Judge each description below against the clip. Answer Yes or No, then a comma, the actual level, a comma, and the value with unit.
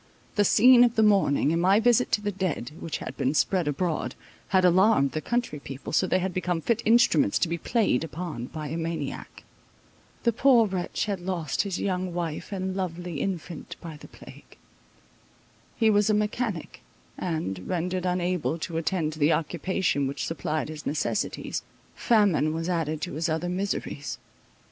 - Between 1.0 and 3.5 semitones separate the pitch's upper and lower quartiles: No, average, 3.9 semitones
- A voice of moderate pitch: Yes, medium, 180 Hz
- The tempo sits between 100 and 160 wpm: No, average, 170 wpm